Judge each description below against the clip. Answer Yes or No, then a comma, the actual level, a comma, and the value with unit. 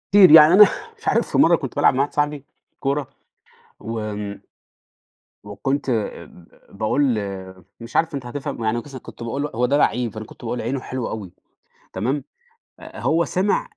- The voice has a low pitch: Yes, low, 130 Hz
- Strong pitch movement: No, average, 4.5 semitones